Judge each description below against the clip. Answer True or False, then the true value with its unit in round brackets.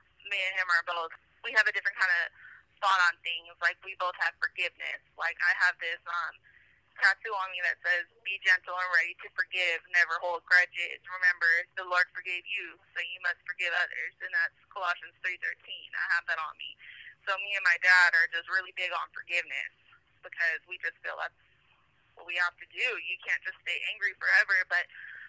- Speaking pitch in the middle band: True (180 Hz)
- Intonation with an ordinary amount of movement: False (1.4 semitones)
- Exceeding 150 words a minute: True (205 wpm)